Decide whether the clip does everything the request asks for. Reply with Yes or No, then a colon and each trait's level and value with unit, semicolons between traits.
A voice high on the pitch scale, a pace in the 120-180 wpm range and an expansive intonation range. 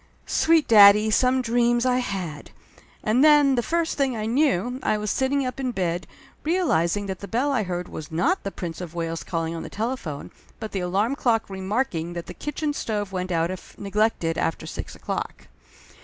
No: high, 215 Hz; average, 190 wpm; wide, 6.4 semitones